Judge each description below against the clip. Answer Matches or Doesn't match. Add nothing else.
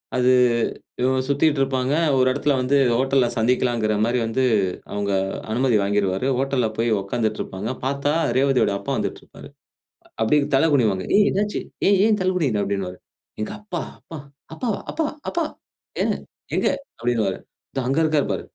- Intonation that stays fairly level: Doesn't match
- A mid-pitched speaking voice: Doesn't match